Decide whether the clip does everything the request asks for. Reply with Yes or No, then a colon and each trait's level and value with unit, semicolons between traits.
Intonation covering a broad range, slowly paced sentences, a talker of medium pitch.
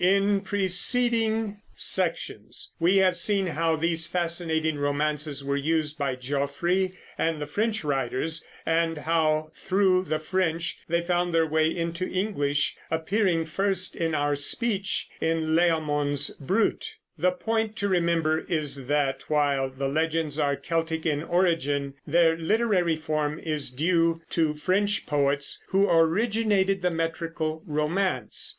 No: average, 3.5 semitones; slow, 130 wpm; medium, 165 Hz